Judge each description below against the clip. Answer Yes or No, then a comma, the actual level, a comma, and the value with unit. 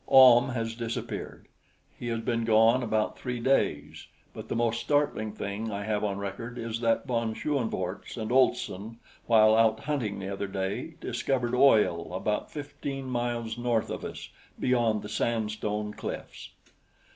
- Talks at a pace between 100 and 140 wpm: No, average, 150 wpm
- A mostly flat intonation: Yes, narrow, 2.3 semitones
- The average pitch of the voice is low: Yes, low, 115 Hz